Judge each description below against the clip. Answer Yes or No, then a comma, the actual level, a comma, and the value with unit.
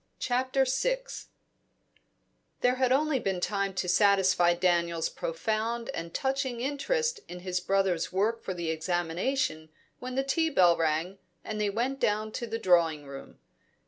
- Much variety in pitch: Yes, wide, 6.7 semitones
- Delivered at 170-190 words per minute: No, average, 145 wpm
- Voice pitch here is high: Yes, high, 200 Hz